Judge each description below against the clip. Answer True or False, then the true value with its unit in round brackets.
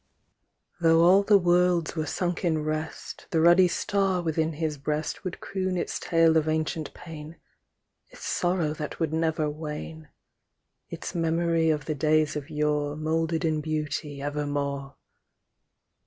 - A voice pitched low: False (160 Hz)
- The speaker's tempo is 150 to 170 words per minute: False (140 wpm)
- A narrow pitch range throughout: True (2.0 semitones)